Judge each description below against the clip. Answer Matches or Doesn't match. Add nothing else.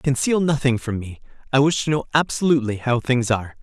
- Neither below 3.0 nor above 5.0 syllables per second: Doesn't match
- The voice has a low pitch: Matches